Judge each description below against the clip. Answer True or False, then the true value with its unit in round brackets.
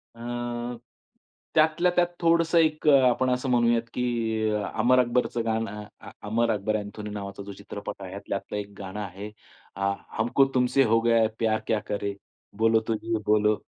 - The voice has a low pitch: True (115 Hz)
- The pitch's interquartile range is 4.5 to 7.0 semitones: False (2.9 semitones)